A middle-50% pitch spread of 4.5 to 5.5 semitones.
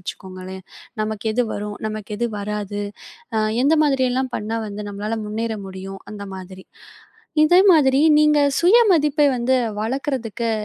Yes: average, 4.9 semitones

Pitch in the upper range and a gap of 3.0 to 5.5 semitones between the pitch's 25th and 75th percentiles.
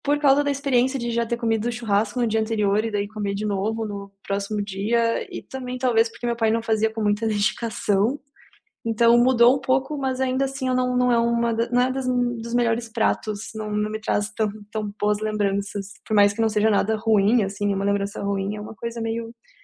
No: high, 225 Hz; narrow, 2.6 semitones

